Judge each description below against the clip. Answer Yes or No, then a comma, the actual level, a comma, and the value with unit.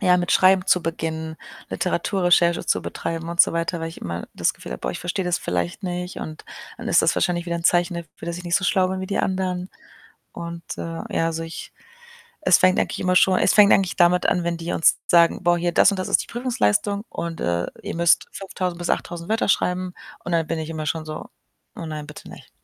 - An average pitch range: No, narrow, 1.9 semitones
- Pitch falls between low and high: Yes, medium, 175 Hz